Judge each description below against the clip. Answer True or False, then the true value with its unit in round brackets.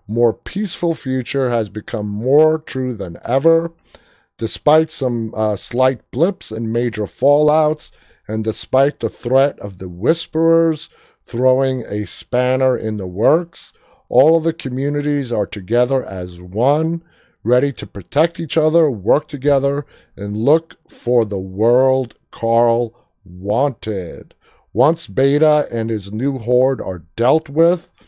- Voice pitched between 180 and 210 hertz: False (130 Hz)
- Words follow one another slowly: True (130 wpm)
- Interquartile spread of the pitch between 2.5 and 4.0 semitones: False (5.2 semitones)